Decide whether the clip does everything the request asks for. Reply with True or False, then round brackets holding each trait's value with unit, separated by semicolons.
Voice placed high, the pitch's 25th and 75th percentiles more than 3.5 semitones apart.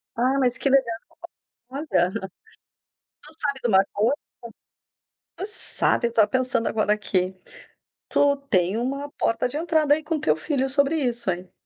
True (255 Hz; 5.1 semitones)